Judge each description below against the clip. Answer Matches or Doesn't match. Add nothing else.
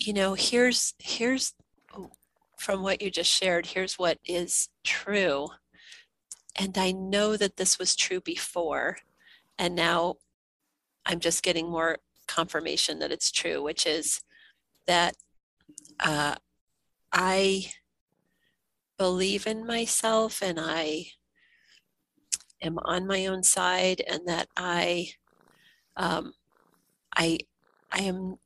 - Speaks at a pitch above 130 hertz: Matches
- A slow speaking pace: Matches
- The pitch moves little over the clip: Doesn't match